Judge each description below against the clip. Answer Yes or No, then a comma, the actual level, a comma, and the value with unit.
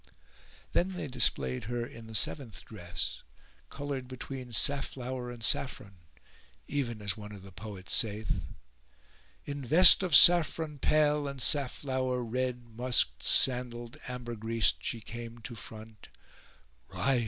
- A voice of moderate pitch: No, low, 120 Hz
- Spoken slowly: Yes, slow, 130 wpm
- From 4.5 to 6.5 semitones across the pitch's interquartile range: No, average, 3.7 semitones